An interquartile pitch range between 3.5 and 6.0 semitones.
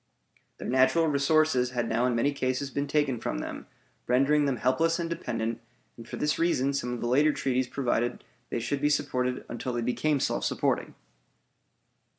No: average, 3.1 semitones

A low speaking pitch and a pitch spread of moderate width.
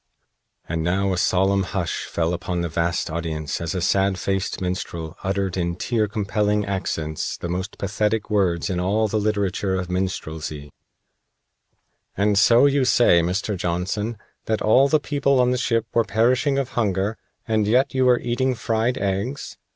Yes: low, 100 Hz; average, 4.0 semitones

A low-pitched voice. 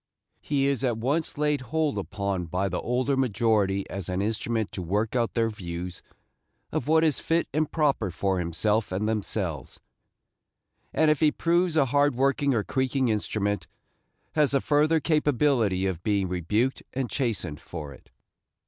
Yes: low, 115 Hz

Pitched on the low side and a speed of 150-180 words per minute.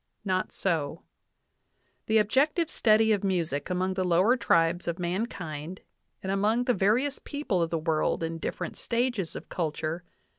No: medium, 185 Hz; average, 155 wpm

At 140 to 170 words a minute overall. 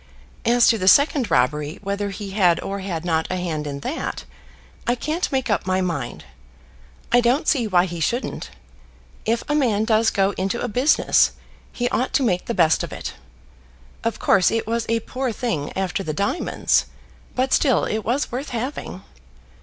No: average, 180 wpm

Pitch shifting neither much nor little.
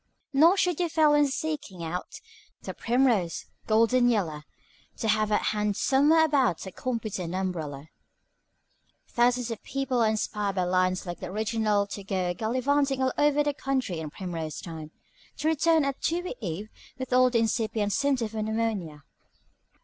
No: wide, 6.4 semitones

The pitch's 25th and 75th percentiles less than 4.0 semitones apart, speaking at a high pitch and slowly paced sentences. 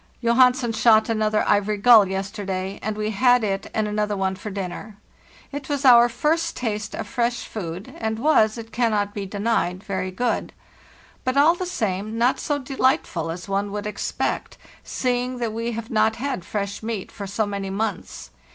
No: average, 3.3 semitones; high, 215 Hz; average, 175 wpm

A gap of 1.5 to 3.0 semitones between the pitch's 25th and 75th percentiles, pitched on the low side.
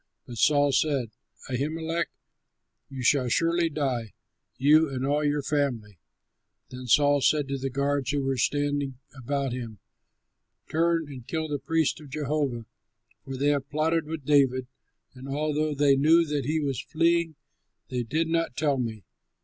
No: average, 2.7 semitones; medium, 145 Hz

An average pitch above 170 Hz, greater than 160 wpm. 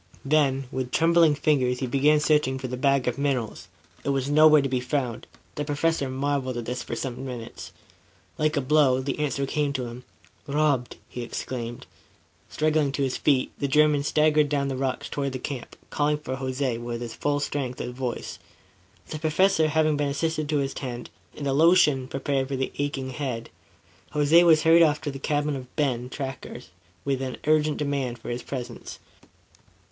No: medium, 140 Hz; average, 185 wpm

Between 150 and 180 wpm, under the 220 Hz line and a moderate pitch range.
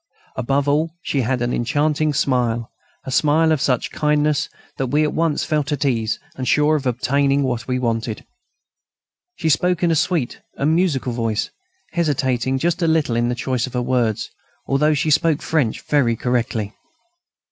Yes: average, 170 wpm; low, 135 Hz; average, 3.7 semitones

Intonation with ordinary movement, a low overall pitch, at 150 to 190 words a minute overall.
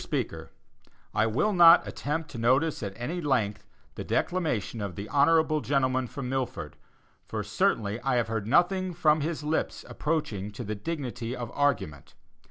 No: wide, 6.0 semitones; low, 130 Hz; average, 160 wpm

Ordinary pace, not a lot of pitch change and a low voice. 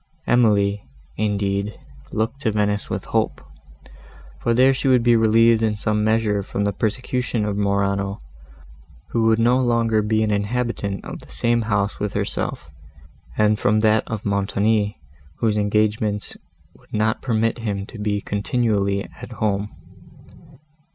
Yes: average, 145 wpm; narrow, 1.9 semitones; low, 105 Hz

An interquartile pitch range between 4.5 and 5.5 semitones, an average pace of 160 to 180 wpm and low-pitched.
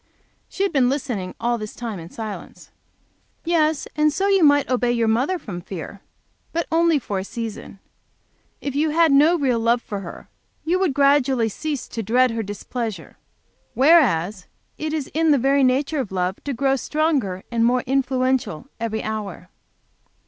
No: average, 5.2 semitones; average, 170 wpm; very high, 255 Hz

